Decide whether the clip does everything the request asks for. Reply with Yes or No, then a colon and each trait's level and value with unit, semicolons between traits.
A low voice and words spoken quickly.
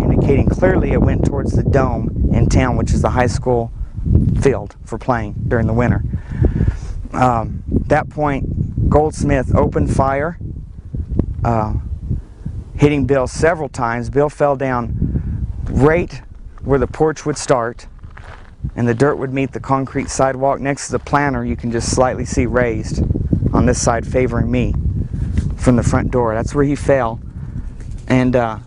No: low, 120 Hz; average, 155 wpm